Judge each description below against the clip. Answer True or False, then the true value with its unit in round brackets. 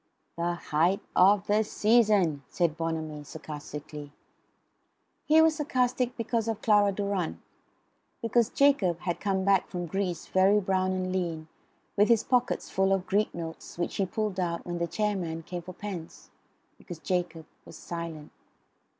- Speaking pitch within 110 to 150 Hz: False (185 Hz)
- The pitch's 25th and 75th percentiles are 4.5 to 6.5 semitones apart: False (3.8 semitones)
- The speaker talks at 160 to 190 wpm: False (150 wpm)